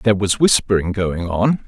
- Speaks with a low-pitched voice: Yes, low, 100 Hz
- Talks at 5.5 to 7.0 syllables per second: No, 4.9 syllables/s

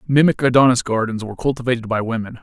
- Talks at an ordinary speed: Yes, average, 175 wpm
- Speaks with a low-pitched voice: Yes, low, 120 Hz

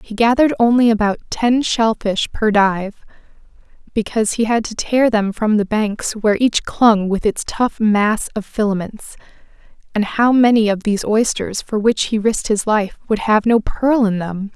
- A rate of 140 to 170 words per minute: No, average, 180 wpm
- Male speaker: No, female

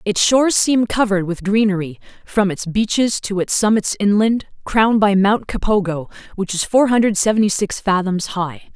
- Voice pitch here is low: No, high, 205 Hz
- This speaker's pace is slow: No, average, 170 wpm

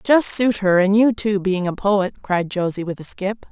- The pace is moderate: No, fast, 240 wpm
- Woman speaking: Yes, female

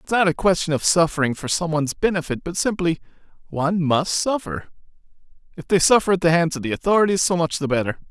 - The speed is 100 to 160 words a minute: No, average, 200 wpm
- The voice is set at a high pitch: No, medium, 170 Hz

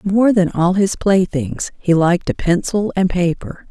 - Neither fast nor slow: Yes, average, 180 wpm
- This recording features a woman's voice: Yes, female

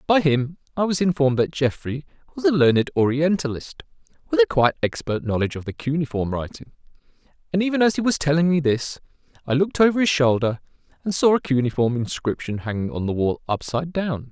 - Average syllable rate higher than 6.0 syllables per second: Yes, 6.2 syllables/s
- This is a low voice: No, medium, 145 Hz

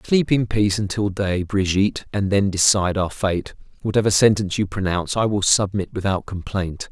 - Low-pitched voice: Yes, low, 100 Hz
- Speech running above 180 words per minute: No, average, 175 wpm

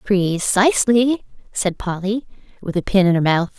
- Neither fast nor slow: Yes, average, 165 wpm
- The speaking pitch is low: No, high, 200 Hz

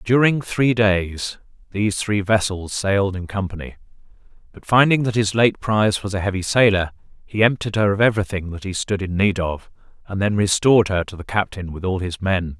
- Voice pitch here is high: No, low, 100 Hz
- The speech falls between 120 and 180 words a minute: No, average, 195 wpm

